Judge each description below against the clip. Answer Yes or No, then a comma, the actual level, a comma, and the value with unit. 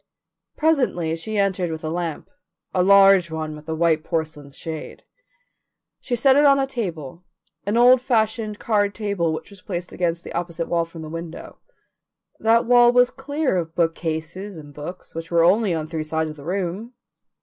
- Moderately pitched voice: Yes, medium, 175 Hz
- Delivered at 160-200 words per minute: Yes, average, 180 wpm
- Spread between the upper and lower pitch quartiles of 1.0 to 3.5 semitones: No, average, 5.2 semitones